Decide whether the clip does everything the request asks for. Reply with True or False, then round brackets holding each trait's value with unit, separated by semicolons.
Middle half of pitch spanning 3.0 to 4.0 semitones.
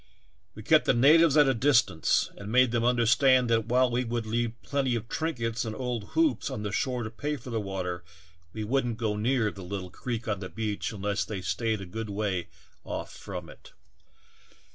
True (3.3 semitones)